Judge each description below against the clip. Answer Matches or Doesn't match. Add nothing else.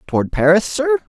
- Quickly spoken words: Doesn't match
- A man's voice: Matches